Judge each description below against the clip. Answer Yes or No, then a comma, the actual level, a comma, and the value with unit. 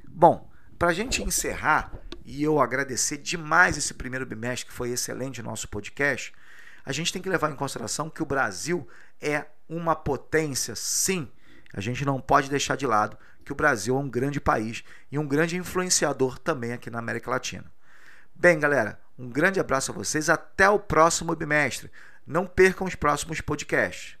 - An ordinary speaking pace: Yes, average, 175 wpm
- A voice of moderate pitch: Yes, medium, 145 Hz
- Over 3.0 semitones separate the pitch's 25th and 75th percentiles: Yes, average, 4.2 semitones